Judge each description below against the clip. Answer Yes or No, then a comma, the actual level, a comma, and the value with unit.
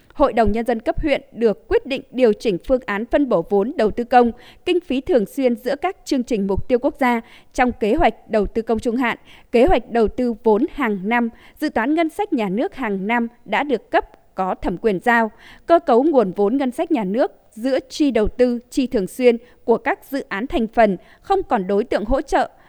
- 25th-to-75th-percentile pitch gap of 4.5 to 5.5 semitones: No, average, 3.8 semitones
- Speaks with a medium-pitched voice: No, high, 245 Hz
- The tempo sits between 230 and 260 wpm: Yes, average, 235 wpm